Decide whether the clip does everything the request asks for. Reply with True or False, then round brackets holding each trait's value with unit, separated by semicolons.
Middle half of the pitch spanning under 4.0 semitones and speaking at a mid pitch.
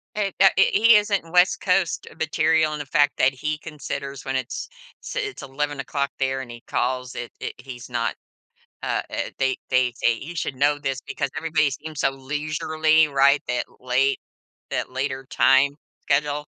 True (2.9 semitones; 145 Hz)